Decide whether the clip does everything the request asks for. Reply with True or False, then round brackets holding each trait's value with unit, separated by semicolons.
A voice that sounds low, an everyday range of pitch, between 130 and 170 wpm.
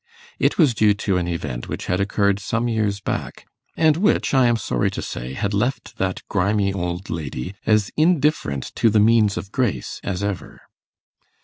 False (100 Hz; 4.2 semitones; 180 wpm)